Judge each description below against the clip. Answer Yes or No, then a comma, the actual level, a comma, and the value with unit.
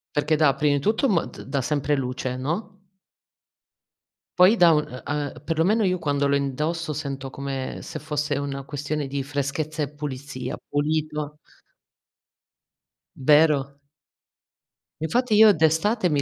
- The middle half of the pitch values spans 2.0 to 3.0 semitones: Yes, narrow, 2.5 semitones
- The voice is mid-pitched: Yes, medium, 150 Hz